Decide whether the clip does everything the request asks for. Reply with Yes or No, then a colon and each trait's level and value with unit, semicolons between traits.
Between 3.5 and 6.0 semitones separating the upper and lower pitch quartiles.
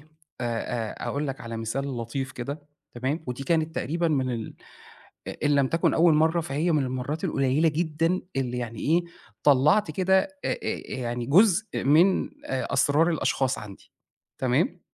Yes: average, 4.0 semitones